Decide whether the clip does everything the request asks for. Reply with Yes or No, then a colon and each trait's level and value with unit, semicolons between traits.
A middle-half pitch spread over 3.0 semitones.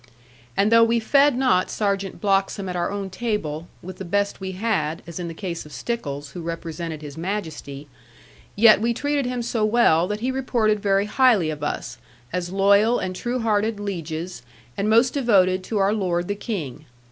Yes: average, 4.7 semitones